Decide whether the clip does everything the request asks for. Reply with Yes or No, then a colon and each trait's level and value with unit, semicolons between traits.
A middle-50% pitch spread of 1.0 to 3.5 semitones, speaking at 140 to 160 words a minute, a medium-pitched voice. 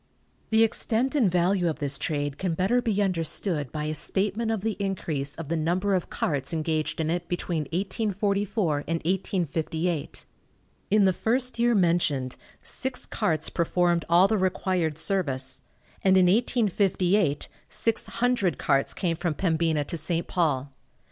No: average, 4.1 semitones; average, 150 wpm; medium, 175 Hz